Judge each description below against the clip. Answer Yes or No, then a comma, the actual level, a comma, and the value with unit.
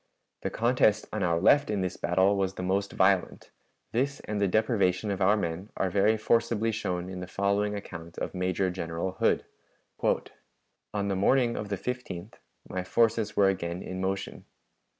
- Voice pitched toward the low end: Yes, low, 100 Hz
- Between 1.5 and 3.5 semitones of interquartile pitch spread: Yes, average, 2.7 semitones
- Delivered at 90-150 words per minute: No, average, 170 wpm